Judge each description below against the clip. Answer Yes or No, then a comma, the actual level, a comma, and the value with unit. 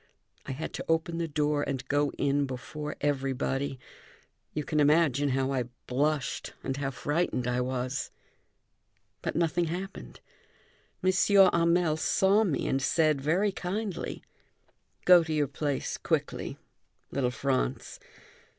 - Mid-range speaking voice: Yes, medium, 150 Hz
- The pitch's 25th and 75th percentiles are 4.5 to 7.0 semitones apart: No, average, 3.9 semitones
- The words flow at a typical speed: No, slow, 130 wpm